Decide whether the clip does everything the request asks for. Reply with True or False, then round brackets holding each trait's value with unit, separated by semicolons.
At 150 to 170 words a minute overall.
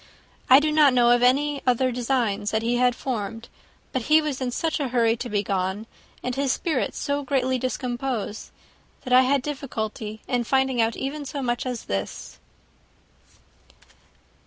True (165 wpm)